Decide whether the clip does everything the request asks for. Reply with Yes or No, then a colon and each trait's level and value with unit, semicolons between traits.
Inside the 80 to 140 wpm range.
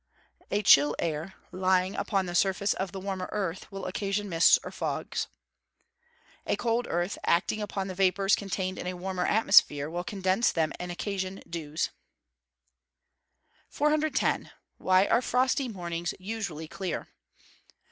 Yes: slow, 135 wpm